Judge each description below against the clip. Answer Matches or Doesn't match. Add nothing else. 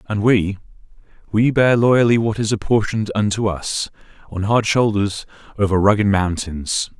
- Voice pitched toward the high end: Doesn't match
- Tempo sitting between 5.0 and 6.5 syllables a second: Doesn't match